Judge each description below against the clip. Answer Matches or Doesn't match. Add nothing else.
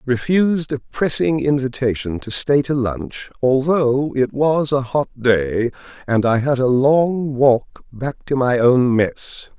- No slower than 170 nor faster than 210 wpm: Doesn't match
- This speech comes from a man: Matches